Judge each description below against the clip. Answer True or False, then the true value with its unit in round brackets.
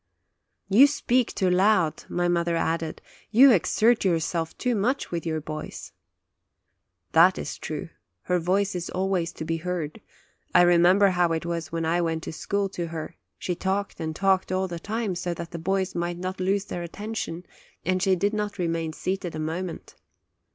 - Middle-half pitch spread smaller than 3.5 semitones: True (2.7 semitones)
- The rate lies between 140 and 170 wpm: False (180 wpm)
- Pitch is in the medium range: True (180 Hz)